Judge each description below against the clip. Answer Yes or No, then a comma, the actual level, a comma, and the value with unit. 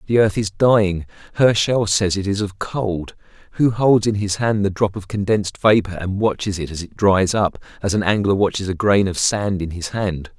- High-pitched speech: No, low, 100 Hz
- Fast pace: Yes, fast, 220 wpm